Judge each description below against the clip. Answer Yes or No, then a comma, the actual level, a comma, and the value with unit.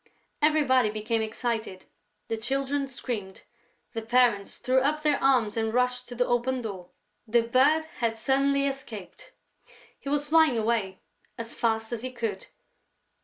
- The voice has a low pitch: No, high, 240 Hz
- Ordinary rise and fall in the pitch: Yes, average, 3.5 semitones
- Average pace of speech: Yes, average, 145 wpm